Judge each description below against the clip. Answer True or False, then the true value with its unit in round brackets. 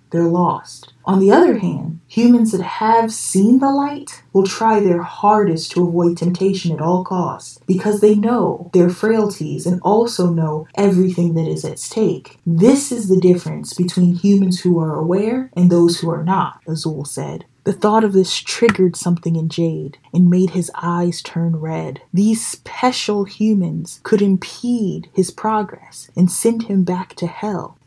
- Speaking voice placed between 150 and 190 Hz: True (185 Hz)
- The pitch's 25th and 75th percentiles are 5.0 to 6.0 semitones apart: False (3.7 semitones)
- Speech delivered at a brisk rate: False (170 wpm)